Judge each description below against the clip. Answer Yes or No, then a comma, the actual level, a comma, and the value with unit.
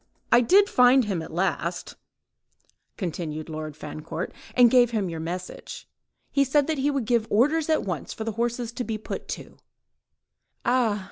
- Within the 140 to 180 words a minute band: Yes, average, 165 wpm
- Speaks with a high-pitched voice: Yes, high, 225 Hz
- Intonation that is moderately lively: No, wide, 6.6 semitones